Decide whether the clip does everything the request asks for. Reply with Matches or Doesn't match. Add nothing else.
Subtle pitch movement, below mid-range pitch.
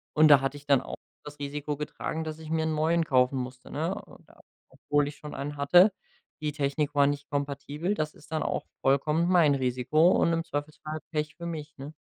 Doesn't match